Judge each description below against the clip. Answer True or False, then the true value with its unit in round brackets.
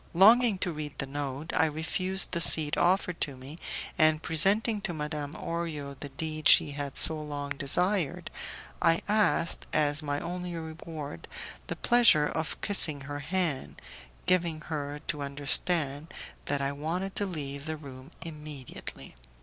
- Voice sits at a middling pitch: True (155 Hz)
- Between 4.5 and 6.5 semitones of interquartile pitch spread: False (3.2 semitones)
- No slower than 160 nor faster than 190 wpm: False (150 wpm)